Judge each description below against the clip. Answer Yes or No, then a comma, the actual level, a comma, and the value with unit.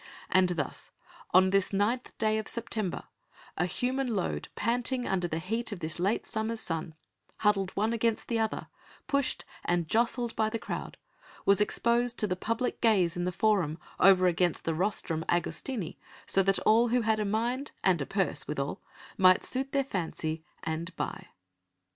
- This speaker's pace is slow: No, average, 170 wpm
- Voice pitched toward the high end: Yes, high, 205 Hz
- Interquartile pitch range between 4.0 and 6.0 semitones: Yes, average, 4.6 semitones